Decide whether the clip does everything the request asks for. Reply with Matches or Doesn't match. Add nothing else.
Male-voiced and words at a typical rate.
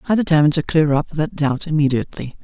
Matches